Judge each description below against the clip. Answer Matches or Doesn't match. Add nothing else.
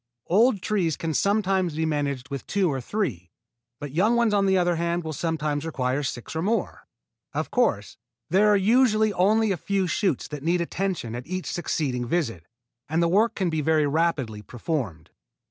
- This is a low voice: Doesn't match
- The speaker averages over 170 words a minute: Matches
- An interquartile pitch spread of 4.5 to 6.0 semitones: Matches